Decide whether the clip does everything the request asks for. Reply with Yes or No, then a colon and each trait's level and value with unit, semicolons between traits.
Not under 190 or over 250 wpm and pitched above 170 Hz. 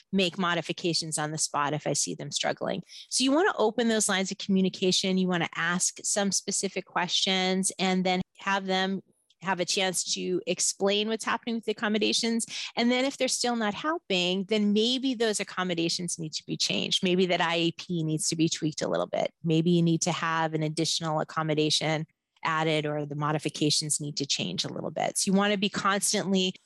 Yes: average, 200 wpm; medium, 185 Hz